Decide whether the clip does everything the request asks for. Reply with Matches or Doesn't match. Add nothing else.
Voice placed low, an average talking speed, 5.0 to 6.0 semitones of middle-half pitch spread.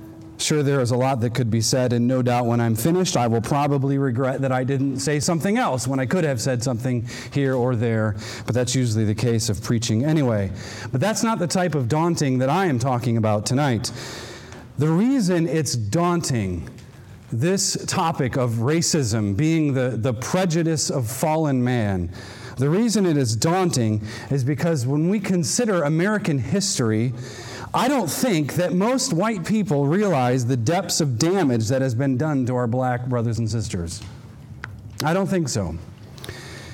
Matches